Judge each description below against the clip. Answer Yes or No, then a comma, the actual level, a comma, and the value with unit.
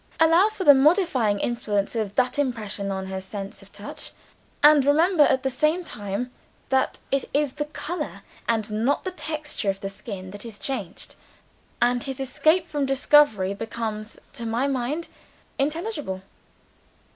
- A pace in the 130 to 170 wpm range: Yes, average, 155 wpm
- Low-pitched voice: No, very high, 255 Hz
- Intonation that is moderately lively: No, wide, 6.1 semitones